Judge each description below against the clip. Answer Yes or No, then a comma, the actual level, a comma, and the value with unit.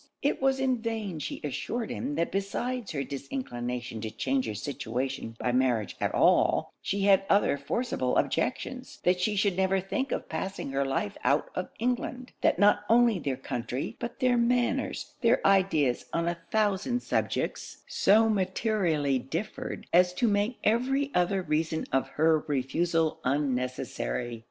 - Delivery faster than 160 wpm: No, average, 155 wpm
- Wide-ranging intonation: Yes, wide, 8.6 semitones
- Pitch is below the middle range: No, medium, 180 Hz